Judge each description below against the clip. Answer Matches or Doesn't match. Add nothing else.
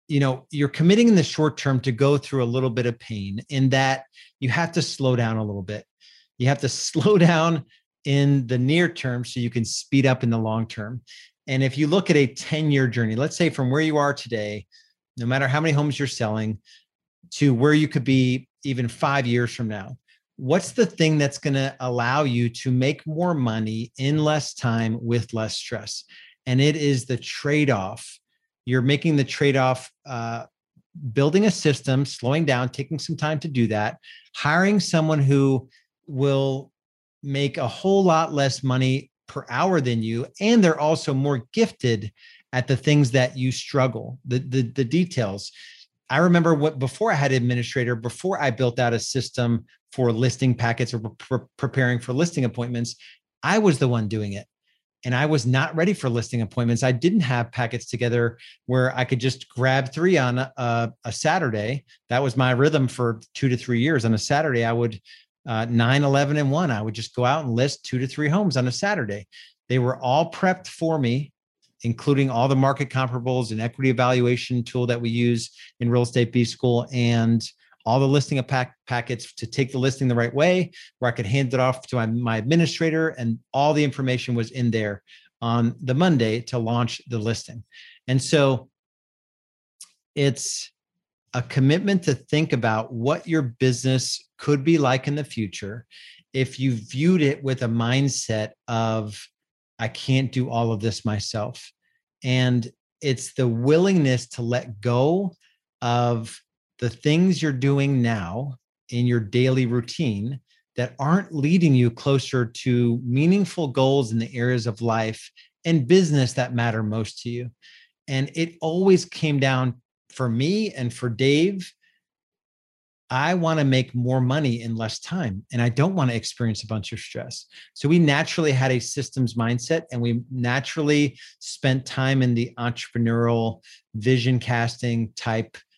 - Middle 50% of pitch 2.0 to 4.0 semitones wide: Matches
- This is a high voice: Doesn't match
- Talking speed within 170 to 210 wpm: Matches